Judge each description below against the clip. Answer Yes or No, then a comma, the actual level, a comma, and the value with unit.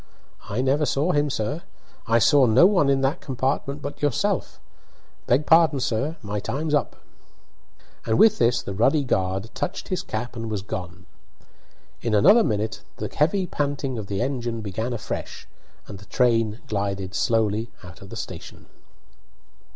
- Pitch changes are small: No, average, 5.3 semitones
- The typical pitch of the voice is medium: No, low, 120 Hz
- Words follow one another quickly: No, average, 160 wpm